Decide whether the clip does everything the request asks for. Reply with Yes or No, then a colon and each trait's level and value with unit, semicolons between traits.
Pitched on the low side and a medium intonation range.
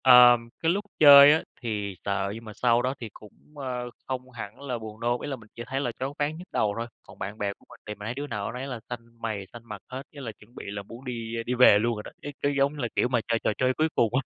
Yes: low, 120 Hz; average, 3.3 semitones